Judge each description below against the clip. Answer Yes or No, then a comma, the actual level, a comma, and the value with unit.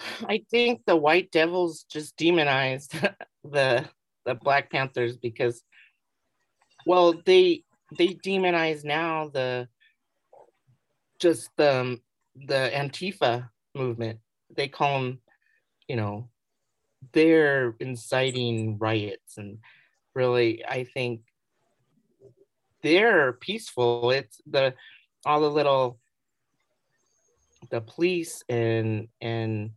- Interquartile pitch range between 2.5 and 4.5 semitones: No, average, 5.2 semitones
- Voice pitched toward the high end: No, low, 135 Hz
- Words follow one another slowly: Yes, slow, 95 wpm